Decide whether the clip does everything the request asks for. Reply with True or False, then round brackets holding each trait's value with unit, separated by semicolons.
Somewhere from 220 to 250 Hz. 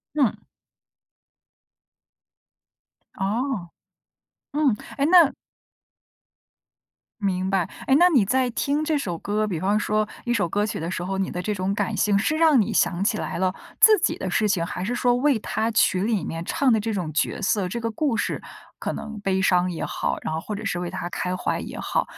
False (210 Hz)